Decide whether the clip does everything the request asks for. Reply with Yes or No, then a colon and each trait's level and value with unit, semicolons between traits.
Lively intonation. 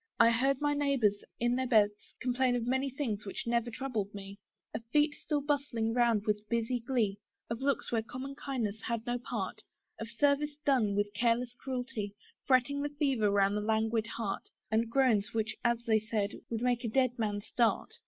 No: average, 3.2 semitones